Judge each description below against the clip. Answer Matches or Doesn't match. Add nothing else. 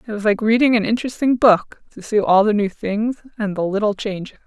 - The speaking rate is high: Matches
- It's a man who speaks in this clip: Doesn't match